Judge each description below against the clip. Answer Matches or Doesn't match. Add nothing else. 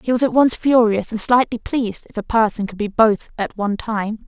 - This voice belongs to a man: Doesn't match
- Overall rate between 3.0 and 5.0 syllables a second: Doesn't match